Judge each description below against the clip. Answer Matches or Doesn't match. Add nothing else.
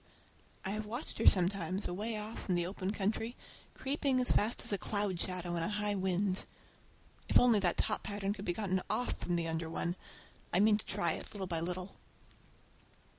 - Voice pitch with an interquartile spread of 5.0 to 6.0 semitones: Doesn't match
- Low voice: Doesn't match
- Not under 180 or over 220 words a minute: Matches